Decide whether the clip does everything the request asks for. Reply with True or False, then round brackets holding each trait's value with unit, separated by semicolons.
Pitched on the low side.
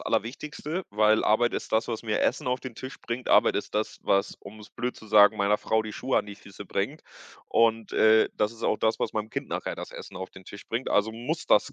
True (110 Hz)